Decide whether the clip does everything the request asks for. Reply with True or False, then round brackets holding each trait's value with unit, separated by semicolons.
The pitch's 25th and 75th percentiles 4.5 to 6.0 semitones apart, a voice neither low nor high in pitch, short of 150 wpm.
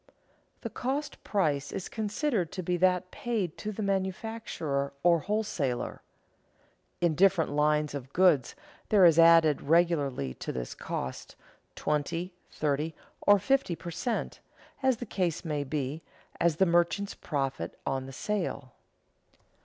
True (5.2 semitones; 170 Hz; 135 wpm)